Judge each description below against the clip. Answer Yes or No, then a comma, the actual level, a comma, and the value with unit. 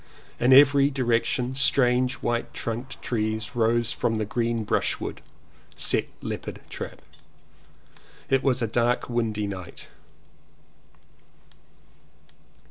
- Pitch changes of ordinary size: No, narrow, 2.3 semitones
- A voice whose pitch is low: Yes, low, 120 Hz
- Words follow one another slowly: Yes, slow, 100 wpm